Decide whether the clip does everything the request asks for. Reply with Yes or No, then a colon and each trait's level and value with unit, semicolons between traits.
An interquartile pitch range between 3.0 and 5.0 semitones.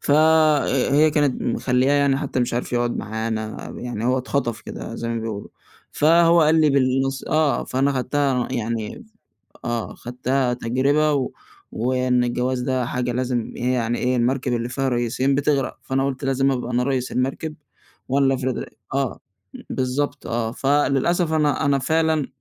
No: narrow, 2.5 semitones